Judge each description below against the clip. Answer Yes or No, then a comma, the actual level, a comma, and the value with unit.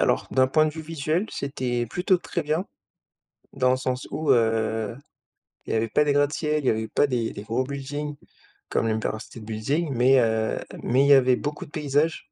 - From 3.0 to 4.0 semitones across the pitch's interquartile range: No, average, 4.6 semitones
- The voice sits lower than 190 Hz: Yes, low, 135 Hz